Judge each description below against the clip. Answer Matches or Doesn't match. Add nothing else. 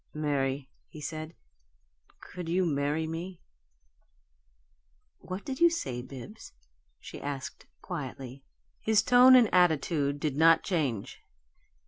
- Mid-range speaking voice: Matches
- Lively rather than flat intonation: Doesn't match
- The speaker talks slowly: Matches